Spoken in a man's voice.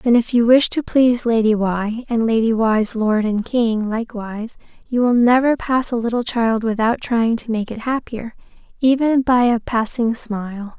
No: female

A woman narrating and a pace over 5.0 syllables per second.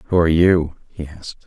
No: male; 5.6 syllables/s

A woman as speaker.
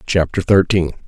No: male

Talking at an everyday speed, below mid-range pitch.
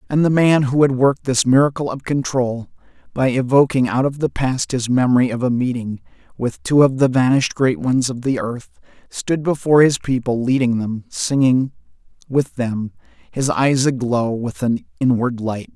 Yes: average, 180 wpm; low, 130 Hz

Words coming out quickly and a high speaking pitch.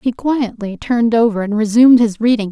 No: average, 190 wpm; high, 230 Hz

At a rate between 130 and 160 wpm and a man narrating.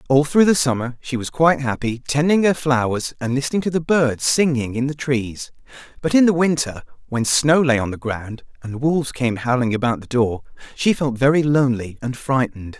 No: average, 200 wpm; male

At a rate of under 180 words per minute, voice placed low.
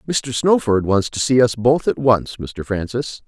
No: average, 200 wpm; low, 120 Hz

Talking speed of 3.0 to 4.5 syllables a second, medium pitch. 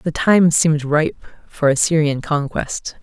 Yes: 4.1 syllables/s; medium, 155 Hz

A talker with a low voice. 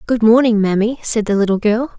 No: high, 220 Hz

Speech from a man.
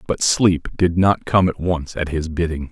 Yes: male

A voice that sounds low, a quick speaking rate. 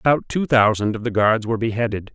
Yes: low, 115 Hz; fast, 225 wpm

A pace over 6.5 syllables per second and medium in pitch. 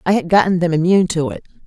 Yes: 7.5 syllables/s; medium, 175 Hz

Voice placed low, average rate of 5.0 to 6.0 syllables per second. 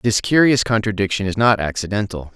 Yes: low, 105 Hz; 5.8 syllables/s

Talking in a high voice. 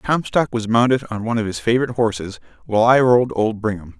No: low, 115 Hz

